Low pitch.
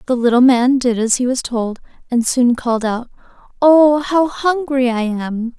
No: very high, 250 Hz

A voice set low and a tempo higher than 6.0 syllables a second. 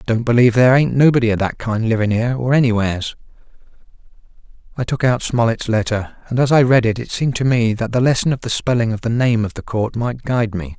Yes: low, 120 Hz; 6.4 syllables/s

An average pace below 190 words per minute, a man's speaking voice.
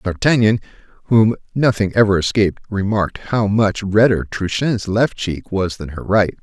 Yes: average, 150 wpm; male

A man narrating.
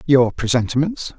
Yes: male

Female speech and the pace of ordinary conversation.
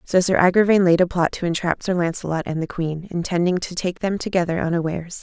No: female; fast, 220 wpm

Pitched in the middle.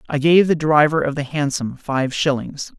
Yes: medium, 145 Hz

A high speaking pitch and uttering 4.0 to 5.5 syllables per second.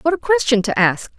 No: high, 220 Hz; 5.8 syllables/s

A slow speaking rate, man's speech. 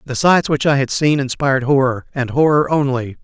No: fast, 205 wpm; male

